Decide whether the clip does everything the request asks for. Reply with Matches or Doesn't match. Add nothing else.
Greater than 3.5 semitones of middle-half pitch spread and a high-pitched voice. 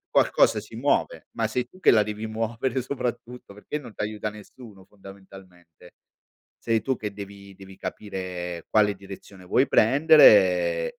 Doesn't match